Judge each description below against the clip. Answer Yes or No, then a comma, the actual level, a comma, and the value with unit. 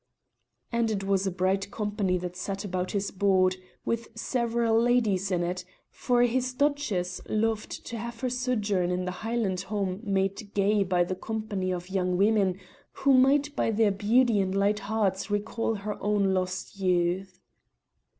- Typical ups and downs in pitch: Yes, average, 3.3 semitones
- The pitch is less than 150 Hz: No, high, 200 Hz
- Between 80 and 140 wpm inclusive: No, average, 160 wpm